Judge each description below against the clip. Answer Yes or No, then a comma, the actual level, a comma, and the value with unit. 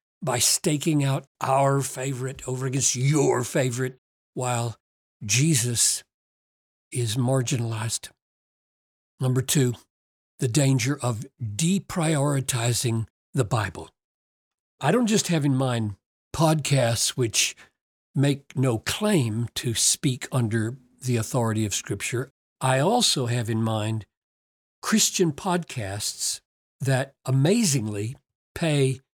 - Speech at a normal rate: No, slow, 100 wpm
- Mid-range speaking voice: No, low, 130 Hz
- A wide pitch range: No, average, 3.3 semitones